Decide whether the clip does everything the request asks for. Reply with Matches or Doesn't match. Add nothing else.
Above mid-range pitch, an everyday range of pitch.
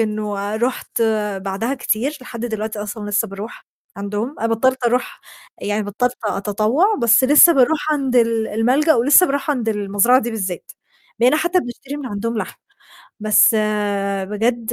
Matches